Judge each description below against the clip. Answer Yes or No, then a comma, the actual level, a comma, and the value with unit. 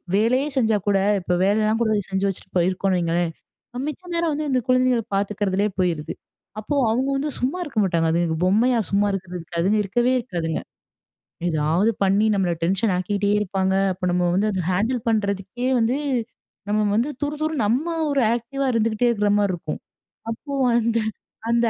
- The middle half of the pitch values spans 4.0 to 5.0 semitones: Yes, average, 4.4 semitones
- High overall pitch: Yes, high, 210 Hz